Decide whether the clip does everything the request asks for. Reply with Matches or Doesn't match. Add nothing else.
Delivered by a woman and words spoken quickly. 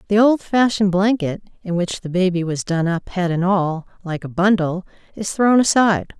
Doesn't match